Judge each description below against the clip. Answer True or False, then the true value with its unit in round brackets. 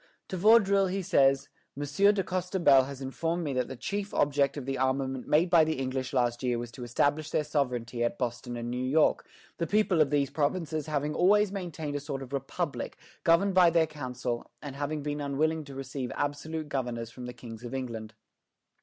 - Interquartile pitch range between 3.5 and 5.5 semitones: True (4.1 semitones)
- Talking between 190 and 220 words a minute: True (200 wpm)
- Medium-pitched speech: True (145 Hz)